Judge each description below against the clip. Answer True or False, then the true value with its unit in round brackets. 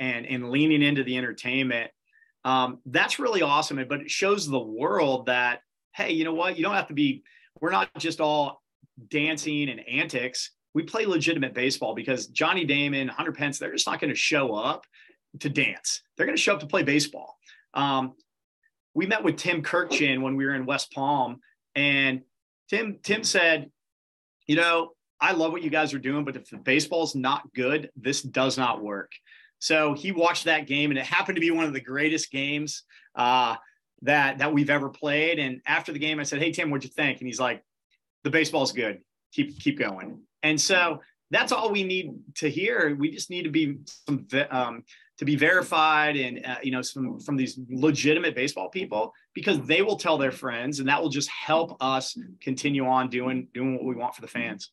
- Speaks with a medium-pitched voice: True (145 Hz)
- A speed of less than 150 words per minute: False (200 wpm)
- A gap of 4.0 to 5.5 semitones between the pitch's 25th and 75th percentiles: False (3.6 semitones)